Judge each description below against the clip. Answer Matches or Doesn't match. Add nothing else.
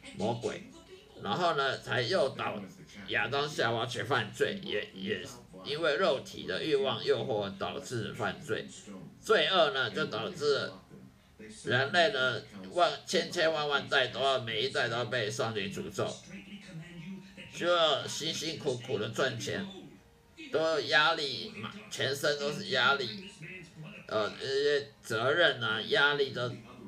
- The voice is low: Doesn't match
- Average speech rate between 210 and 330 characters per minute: Doesn't match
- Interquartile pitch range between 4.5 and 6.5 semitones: Matches